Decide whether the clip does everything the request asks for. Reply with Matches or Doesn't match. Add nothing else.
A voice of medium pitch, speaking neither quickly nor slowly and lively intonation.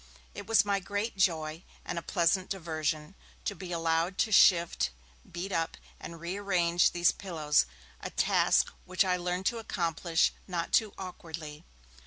Doesn't match